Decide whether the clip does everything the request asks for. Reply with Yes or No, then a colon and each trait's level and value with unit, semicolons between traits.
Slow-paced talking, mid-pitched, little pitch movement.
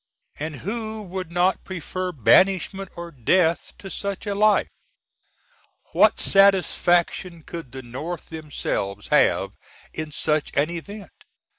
No: slow, 120 wpm; medium, 175 Hz; average, 4.1 semitones